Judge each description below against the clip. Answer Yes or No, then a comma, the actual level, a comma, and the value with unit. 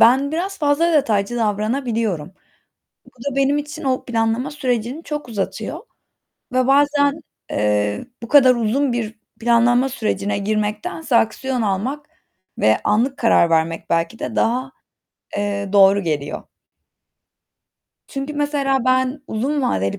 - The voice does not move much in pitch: No, average, 5.1 semitones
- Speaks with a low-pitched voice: No, high, 240 Hz